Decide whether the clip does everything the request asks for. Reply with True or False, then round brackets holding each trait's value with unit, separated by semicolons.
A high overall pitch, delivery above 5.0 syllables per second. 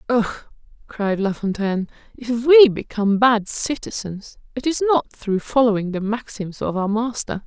False (225 Hz; 4.6 syllables/s)